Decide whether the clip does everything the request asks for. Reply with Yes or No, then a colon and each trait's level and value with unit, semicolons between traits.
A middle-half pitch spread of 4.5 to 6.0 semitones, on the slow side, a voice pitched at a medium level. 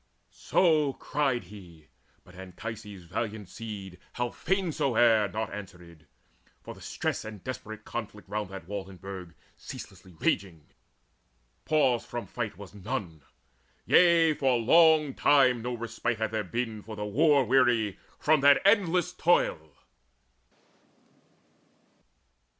No: wide, 5.5 semitones; slow, 125 wpm; low, 110 Hz